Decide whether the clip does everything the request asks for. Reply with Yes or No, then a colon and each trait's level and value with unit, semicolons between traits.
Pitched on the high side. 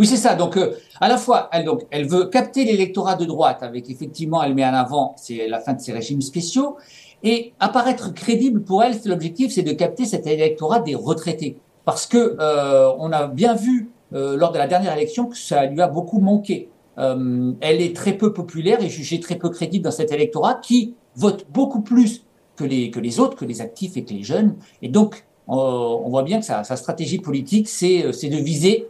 No: medium, 180 Hz